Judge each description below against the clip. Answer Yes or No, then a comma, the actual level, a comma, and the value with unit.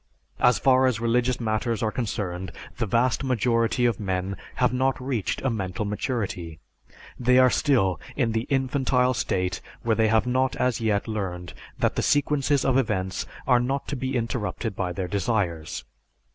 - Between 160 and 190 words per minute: Yes, average, 165 wpm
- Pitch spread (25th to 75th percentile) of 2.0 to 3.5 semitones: No, average, 4.1 semitones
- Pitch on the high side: No, low, 115 Hz